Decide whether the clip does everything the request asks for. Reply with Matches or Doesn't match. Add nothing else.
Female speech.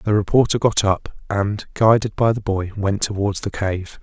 Doesn't match